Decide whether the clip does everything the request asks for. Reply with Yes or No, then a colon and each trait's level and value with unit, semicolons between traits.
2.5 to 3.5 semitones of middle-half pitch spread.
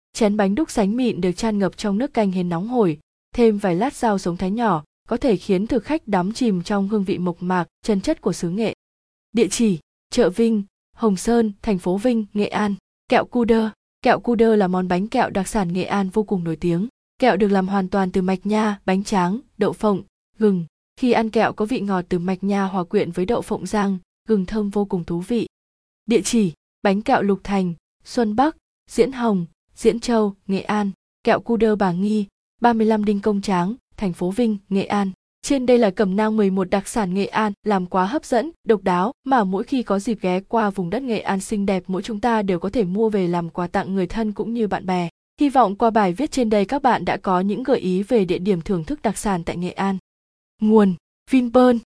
Yes: average, 3.2 semitones